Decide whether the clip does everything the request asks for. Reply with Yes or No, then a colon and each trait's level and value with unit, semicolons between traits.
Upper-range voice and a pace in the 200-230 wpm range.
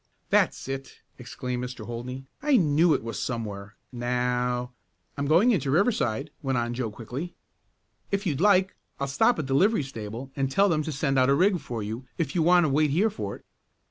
No: low, 135 Hz; fast, 205 wpm